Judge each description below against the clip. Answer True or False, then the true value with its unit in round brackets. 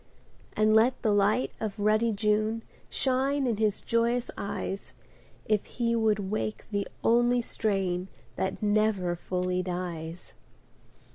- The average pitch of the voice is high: True (215 Hz)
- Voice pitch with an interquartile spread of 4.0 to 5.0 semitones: False (3.1 semitones)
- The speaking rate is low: True (125 wpm)